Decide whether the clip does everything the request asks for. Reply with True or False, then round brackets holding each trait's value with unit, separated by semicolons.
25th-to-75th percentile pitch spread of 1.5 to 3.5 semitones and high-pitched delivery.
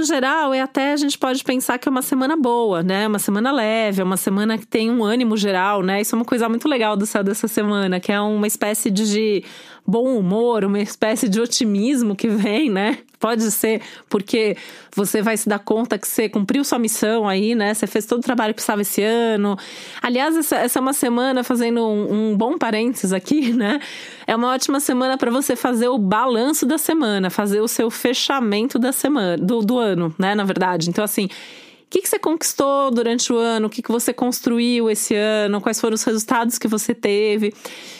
True (3.2 semitones; 230 Hz)